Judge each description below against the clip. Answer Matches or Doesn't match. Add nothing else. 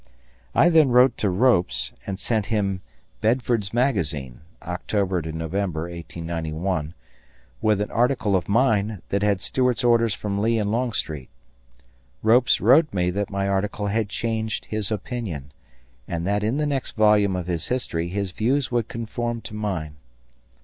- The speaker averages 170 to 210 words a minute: Doesn't match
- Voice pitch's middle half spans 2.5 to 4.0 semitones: Doesn't match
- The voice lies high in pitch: Doesn't match